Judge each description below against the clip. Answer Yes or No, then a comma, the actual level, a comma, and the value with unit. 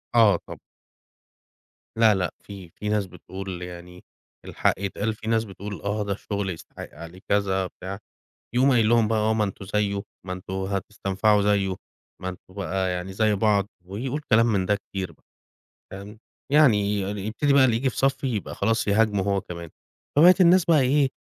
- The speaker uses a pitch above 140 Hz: No, low, 100 Hz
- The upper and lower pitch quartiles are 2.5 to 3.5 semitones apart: Yes, average, 2.9 semitones